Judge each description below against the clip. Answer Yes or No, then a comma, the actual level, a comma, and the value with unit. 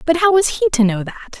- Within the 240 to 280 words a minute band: No, fast, 300 wpm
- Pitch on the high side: Yes, very high, 280 Hz